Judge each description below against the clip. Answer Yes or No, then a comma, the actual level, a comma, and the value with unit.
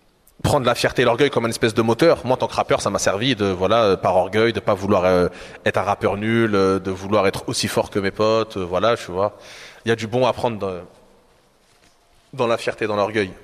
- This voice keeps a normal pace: No, fast, 235 wpm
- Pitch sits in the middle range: No, low, 110 Hz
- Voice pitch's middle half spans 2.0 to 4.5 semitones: Yes, average, 3.3 semitones